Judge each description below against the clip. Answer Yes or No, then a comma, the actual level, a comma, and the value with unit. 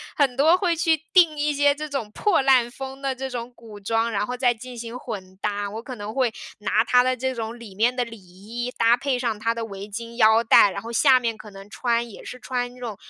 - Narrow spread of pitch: No, average, 3.0 semitones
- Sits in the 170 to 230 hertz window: No, high, 240 Hz